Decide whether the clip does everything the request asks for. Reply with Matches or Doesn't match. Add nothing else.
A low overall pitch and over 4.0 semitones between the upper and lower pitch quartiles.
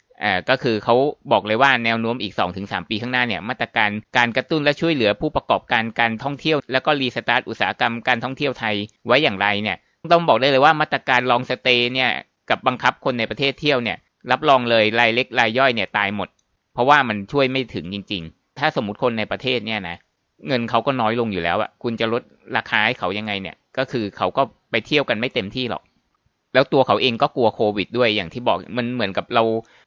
Doesn't match